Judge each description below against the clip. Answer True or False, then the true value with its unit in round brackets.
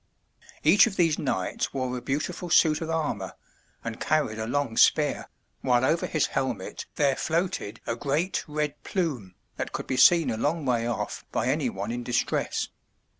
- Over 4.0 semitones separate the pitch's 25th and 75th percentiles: True (5.2 semitones)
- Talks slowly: False (175 wpm)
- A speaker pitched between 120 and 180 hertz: True (140 Hz)